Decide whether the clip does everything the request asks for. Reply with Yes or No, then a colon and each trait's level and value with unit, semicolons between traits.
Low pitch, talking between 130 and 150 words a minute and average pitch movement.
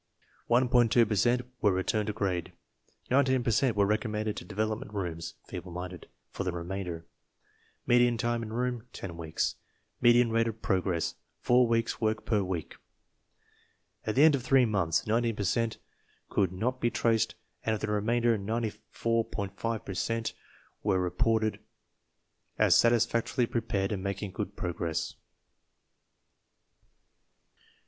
Yes: low, 110 Hz; average, 140 wpm; average, 3.3 semitones